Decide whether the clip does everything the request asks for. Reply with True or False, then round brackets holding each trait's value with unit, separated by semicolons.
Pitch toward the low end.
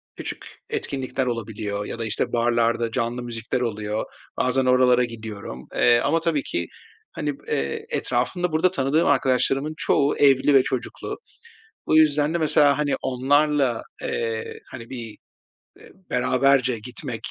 True (125 Hz)